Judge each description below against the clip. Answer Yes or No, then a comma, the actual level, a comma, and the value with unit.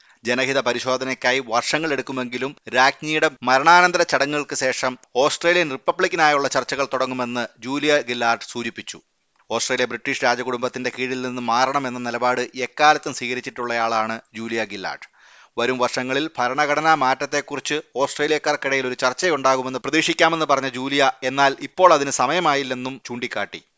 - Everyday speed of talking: Yes, average, 105 wpm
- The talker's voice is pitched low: Yes, low, 130 Hz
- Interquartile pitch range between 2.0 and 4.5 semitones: Yes, narrow, 2.5 semitones